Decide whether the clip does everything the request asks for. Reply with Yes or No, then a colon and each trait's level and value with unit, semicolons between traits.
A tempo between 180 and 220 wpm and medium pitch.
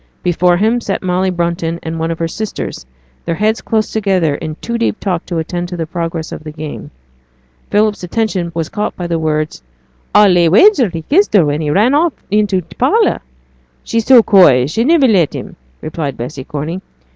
Yes: average, 200 wpm; medium, 175 Hz